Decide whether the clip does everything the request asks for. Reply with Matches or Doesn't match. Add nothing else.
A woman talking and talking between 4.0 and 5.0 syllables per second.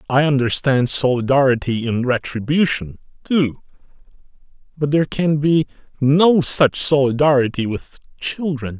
Doesn't match